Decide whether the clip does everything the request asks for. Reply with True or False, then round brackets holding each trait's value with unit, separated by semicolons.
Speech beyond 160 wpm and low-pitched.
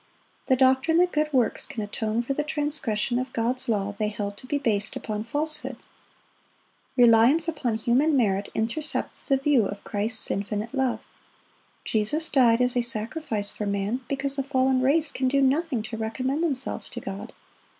False (170 wpm; 255 Hz)